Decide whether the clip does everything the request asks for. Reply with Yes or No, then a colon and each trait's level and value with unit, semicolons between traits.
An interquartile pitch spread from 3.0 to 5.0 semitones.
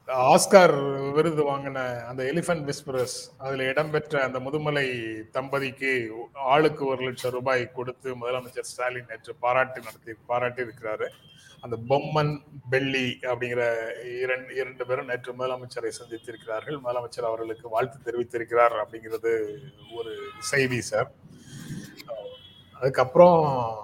No: narrow, 2.6 semitones